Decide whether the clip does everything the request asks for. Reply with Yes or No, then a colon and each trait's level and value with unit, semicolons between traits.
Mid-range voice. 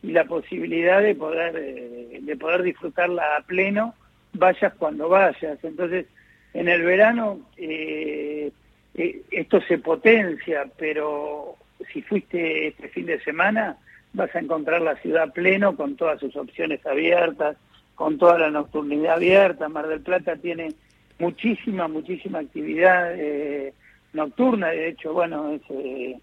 Yes: medium, 165 Hz